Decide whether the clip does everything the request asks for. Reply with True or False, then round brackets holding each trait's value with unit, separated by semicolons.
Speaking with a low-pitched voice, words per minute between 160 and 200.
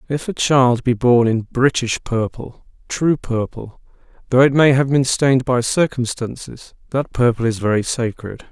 False (125 Hz; 150 wpm)